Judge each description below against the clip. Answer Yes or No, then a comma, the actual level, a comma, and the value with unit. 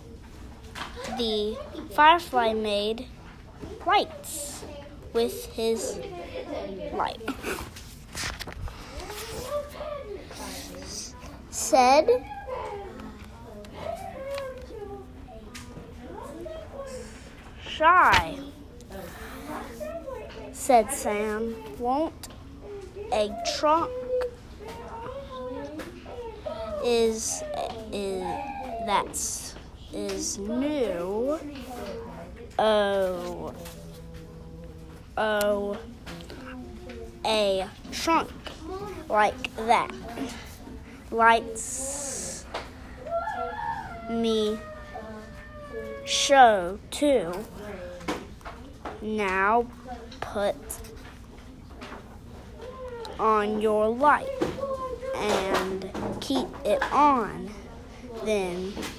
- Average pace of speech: No, slow, 40 wpm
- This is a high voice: Yes, high, 230 Hz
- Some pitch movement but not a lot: No, wide, 7.7 semitones